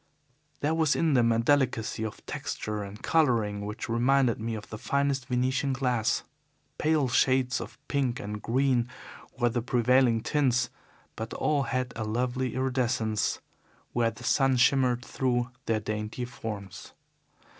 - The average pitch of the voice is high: No, low, 125 Hz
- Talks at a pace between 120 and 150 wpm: Yes, average, 145 wpm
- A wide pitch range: No, average, 2.8 semitones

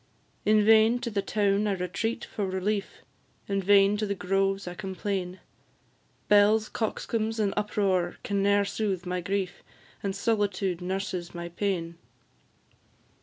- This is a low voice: No, high, 200 Hz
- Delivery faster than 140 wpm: No, slow, 135 wpm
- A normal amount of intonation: No, narrow, 2.1 semitones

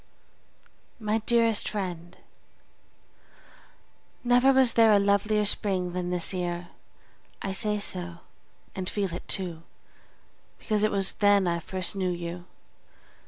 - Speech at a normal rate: No, slow, 120 wpm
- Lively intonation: No, average, 3.0 semitones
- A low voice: No, high, 195 Hz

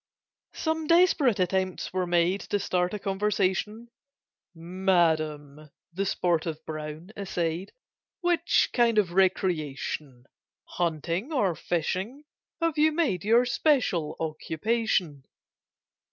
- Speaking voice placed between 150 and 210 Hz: Yes, medium, 185 Hz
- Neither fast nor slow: No, slow, 100 wpm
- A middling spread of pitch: No, wide, 5.7 semitones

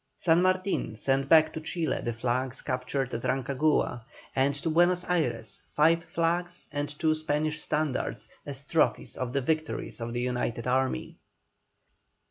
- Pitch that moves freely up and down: No, average, 4.1 semitones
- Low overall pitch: No, medium, 145 Hz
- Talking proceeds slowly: No, average, 145 wpm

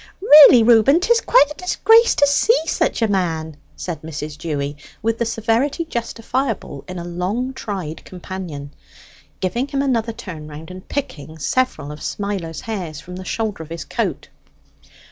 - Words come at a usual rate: Yes, average, 160 wpm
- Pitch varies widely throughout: Yes, wide, 7.9 semitones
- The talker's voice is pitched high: Yes, high, 200 Hz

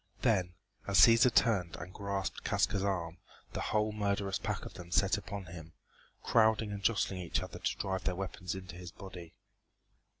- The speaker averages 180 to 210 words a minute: No, average, 170 wpm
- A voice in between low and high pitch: No, very low, 95 Hz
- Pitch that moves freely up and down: No, narrow, 2.4 semitones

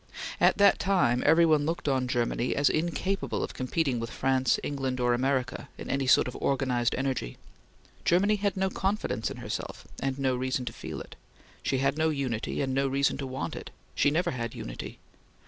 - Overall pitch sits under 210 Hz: Yes, low, 135 Hz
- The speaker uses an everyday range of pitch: Yes, average, 3.8 semitones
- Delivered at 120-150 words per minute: No, average, 185 wpm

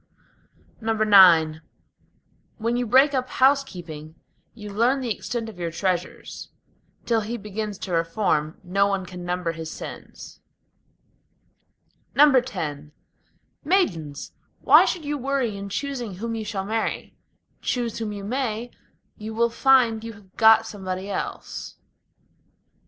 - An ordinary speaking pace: No, slow, 125 wpm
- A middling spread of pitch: Yes, average, 4.6 semitones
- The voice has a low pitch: No, high, 215 Hz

